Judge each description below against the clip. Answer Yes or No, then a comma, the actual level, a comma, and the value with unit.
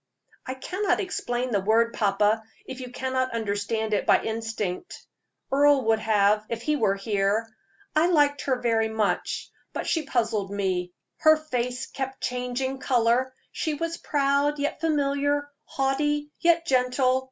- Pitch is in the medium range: No, very high, 255 Hz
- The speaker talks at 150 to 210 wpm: No, average, 140 wpm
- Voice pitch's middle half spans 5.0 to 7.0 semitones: No, average, 4.5 semitones